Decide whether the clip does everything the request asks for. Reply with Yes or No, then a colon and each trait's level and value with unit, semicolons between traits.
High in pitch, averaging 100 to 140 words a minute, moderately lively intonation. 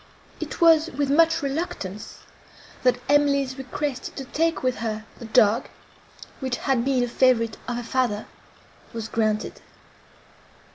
Yes: very high, 255 Hz; slow, 135 wpm; average, 3.7 semitones